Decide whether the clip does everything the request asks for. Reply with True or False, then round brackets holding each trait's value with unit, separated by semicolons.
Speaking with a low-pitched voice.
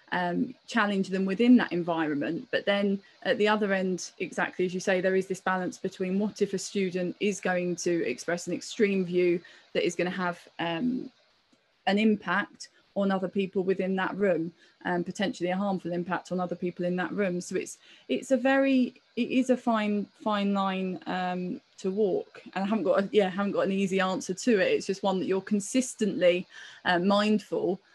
False (190 Hz)